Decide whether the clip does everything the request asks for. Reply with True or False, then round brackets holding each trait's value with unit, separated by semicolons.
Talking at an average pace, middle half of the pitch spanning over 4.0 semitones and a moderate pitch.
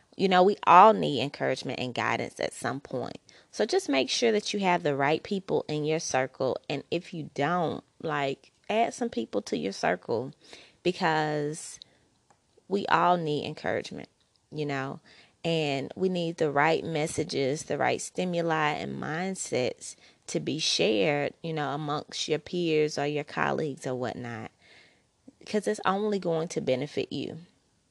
False (155 wpm; 3.5 semitones; 155 Hz)